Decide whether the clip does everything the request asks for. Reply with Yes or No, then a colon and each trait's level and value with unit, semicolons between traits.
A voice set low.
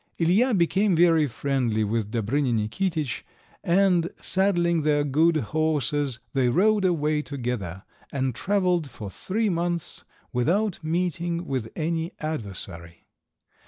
No: medium, 155 Hz